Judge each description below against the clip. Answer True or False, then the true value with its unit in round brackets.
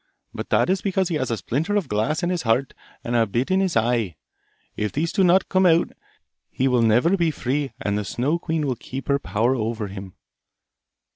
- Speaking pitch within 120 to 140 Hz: True (135 Hz)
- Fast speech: True (215 wpm)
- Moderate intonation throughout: False (7.0 semitones)